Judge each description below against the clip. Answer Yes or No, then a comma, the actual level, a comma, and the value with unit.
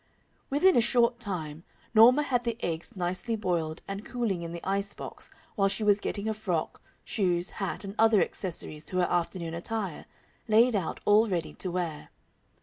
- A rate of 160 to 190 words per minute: Yes, average, 175 wpm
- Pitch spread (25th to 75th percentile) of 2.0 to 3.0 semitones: No, average, 4.3 semitones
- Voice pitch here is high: Yes, high, 195 Hz